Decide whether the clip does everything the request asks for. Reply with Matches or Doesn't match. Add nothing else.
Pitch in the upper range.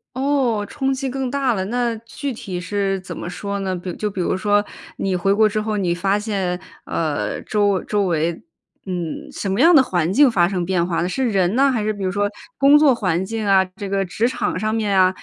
Matches